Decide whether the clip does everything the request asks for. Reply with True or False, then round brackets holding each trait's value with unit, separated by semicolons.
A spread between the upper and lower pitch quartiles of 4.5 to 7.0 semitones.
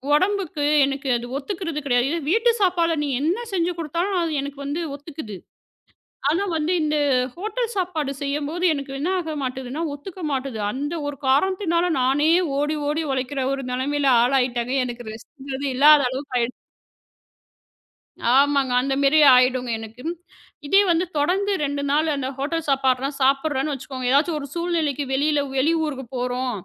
False (3.7 semitones)